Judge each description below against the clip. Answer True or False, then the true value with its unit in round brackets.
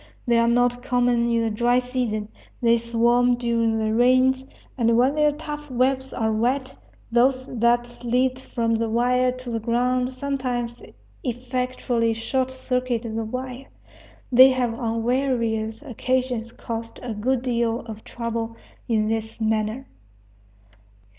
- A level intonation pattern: True (1.8 semitones)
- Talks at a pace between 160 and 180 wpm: False (140 wpm)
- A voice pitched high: True (240 Hz)